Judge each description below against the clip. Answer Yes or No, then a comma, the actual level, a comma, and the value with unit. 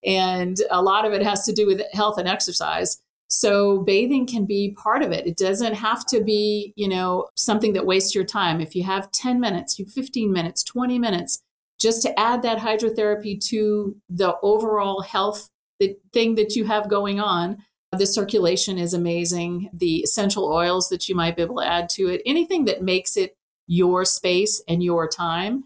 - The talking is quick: No, average, 190 wpm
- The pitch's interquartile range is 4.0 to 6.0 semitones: No, average, 2.9 semitones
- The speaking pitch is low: No, high, 200 Hz